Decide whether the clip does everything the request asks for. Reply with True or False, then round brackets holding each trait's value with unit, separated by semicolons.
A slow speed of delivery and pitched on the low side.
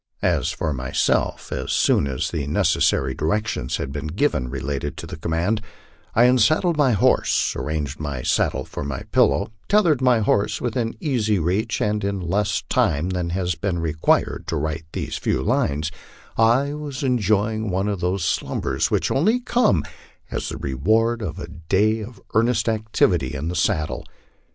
False (165 wpm; 95 Hz)